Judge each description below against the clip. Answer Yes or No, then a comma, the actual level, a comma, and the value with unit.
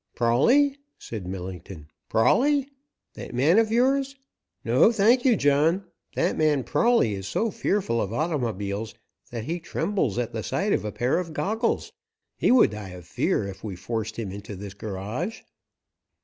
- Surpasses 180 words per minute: No, average, 160 wpm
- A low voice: Yes, low, 125 Hz